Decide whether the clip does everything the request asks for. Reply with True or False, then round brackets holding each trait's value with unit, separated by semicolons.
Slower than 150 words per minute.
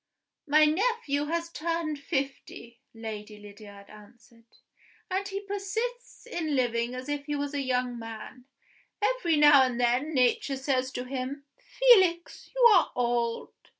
True (140 wpm)